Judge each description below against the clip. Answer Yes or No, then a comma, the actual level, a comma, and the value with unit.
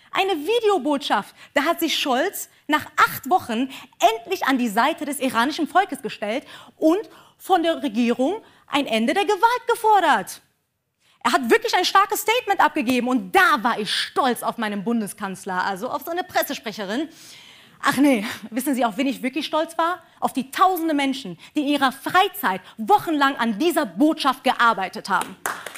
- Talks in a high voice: Yes, very high, 290 Hz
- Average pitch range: No, wide, 6.5 semitones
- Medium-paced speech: Yes, average, 160 wpm